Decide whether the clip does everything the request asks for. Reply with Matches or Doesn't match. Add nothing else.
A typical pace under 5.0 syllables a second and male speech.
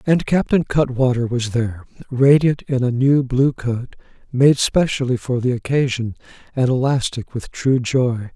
Matches